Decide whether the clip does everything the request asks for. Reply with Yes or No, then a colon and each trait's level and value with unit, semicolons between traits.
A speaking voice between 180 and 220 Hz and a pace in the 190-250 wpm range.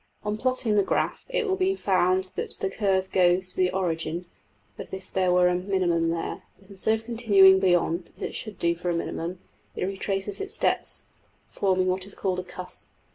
Yes: high, 190 Hz; fast, 205 wpm